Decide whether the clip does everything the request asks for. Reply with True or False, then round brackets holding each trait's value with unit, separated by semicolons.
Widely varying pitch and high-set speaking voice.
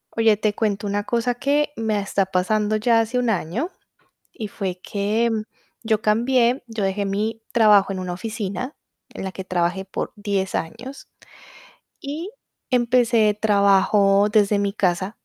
False (2.8 semitones; 210 Hz)